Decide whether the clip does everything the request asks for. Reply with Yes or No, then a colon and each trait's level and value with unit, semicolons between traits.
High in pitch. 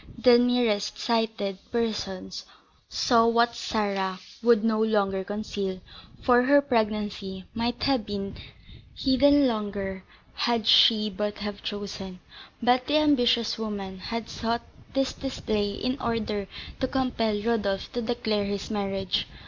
Yes: high, 220 Hz